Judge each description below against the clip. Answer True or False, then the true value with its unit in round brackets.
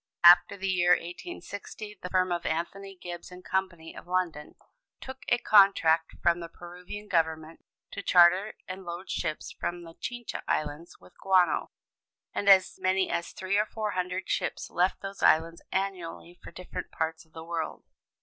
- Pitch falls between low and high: True (180 Hz)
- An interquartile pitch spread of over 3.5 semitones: False (2.4 semitones)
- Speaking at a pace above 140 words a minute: True (165 wpm)